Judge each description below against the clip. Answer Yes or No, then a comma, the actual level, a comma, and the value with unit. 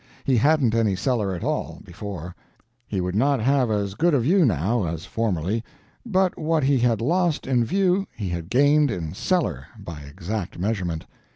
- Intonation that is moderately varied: No, wide, 7.5 semitones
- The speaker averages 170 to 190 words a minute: Yes, average, 175 wpm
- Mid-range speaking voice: No, low, 115 Hz